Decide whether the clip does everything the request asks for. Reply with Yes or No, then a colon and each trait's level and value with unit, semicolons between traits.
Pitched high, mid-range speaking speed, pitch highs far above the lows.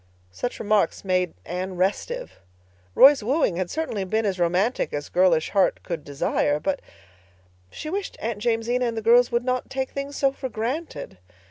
Yes: high, 215 Hz; average, 160 wpm; wide, 6.2 semitones